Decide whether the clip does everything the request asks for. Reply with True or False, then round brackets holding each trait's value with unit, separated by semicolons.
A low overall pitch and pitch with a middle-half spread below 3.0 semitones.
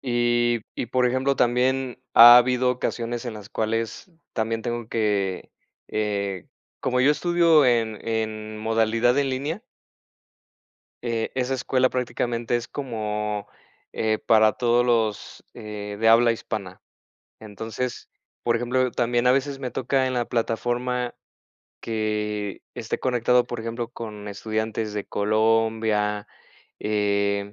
True (115 Hz; 2.5 semitones)